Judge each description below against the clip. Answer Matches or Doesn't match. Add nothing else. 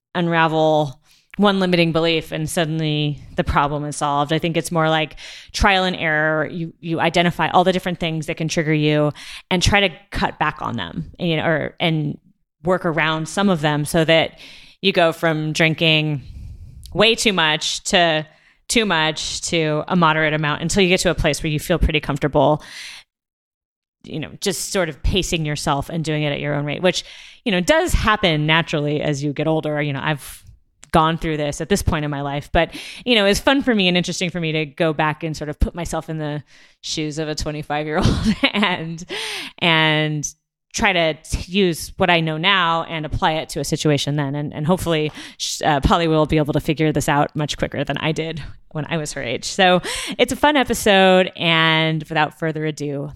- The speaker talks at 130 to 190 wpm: Doesn't match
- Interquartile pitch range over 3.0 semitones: Doesn't match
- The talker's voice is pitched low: Doesn't match